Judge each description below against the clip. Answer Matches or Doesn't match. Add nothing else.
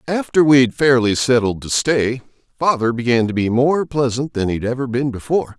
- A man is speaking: Matches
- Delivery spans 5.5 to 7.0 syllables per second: Doesn't match